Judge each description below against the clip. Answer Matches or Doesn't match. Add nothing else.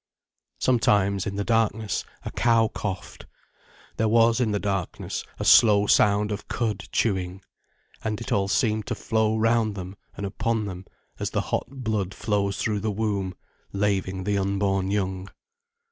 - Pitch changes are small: Matches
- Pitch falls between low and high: Doesn't match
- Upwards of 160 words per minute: Doesn't match